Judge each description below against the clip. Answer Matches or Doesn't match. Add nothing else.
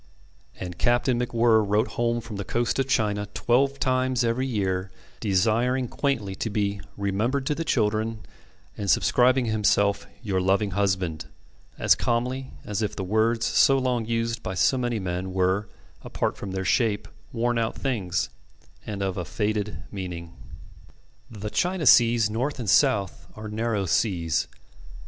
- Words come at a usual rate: Matches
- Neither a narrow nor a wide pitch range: Matches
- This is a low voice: Matches